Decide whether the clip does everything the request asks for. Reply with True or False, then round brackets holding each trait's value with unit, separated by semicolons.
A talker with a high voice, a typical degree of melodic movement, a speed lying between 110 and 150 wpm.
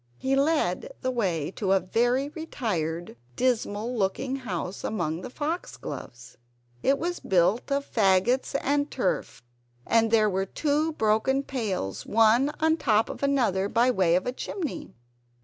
False (230 Hz; 6.3 semitones; 145 wpm)